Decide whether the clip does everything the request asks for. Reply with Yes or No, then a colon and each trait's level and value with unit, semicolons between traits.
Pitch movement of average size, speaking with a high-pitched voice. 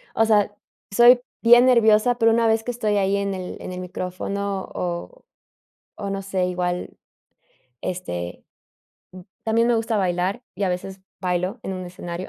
Yes: average, 3.6 semitones; high, 195 Hz